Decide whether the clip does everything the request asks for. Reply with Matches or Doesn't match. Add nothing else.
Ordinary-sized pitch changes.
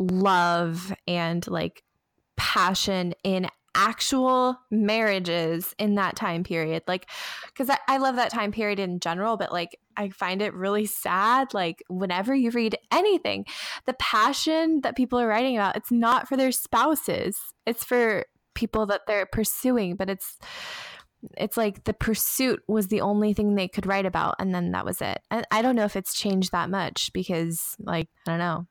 Matches